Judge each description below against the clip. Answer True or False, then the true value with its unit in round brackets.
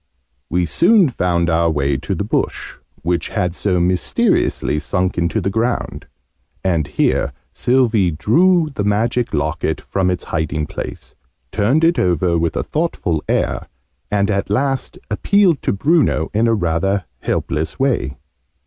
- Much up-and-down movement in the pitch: True (6.2 semitones)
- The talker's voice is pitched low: True (95 Hz)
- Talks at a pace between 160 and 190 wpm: False (145 wpm)